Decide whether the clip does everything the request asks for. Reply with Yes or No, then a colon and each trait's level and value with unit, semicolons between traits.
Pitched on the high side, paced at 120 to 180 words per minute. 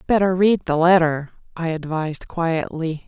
No: medium, 170 Hz; slow, 135 wpm